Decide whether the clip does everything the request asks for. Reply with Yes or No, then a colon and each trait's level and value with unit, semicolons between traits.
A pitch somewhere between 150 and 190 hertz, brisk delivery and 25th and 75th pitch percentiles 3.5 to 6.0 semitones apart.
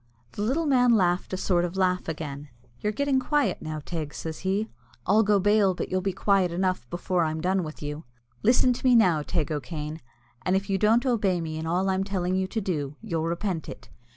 Yes: medium, 185 Hz; fast, 215 wpm; average, 4.2 semitones